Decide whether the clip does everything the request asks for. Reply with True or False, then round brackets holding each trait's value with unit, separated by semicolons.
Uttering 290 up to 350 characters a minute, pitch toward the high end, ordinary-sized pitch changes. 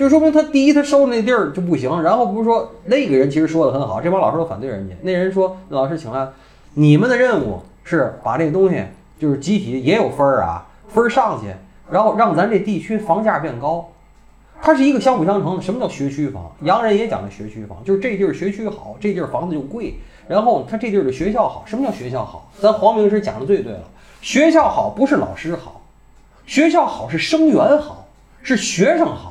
False (330 characters per minute; 200 Hz; 8.8 semitones)